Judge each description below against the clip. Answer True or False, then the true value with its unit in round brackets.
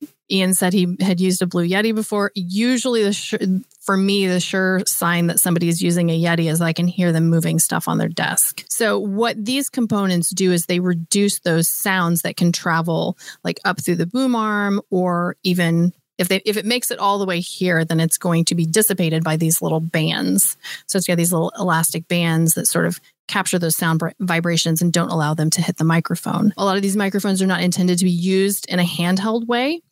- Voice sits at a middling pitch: True (180 Hz)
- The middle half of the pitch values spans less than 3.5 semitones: True (2.9 semitones)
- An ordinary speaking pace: False (225 wpm)